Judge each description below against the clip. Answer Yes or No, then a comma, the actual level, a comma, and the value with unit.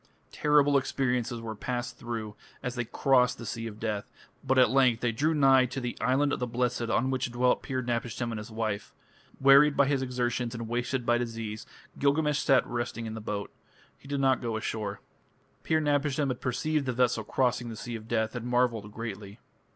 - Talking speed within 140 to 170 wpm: No, average, 195 wpm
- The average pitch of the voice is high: No, low, 120 Hz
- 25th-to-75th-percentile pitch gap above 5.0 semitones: No, average, 2.7 semitones